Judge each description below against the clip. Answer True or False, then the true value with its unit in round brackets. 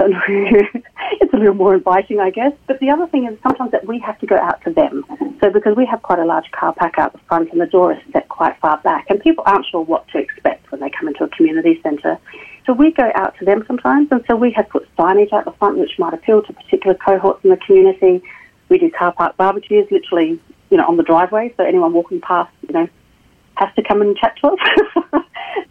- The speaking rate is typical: False (245 wpm)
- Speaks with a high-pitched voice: True (240 Hz)